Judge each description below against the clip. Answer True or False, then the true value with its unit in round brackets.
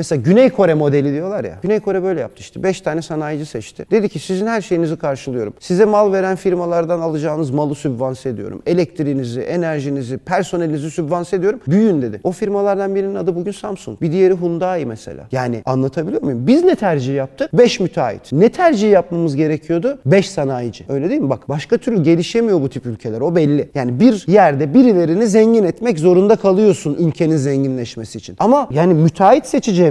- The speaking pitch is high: False (170 Hz)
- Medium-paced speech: False (175 wpm)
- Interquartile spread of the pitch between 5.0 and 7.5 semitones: True (5.5 semitones)